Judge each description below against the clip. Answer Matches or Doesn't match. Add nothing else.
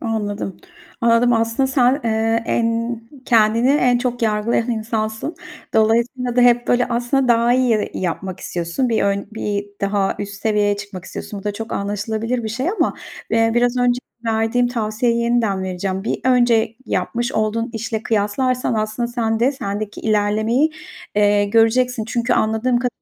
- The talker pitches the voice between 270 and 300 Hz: Doesn't match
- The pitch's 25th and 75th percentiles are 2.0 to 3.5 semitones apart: Matches